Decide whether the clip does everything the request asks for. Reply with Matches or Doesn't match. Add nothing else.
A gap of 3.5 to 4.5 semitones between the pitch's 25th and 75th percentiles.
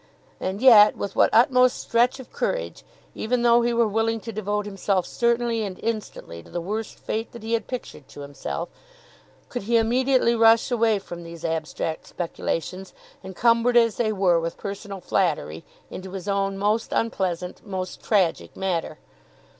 Matches